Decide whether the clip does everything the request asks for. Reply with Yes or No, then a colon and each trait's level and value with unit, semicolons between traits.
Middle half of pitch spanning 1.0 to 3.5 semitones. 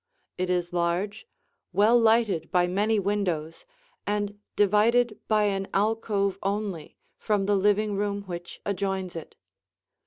Yes: narrow, 2.4 semitones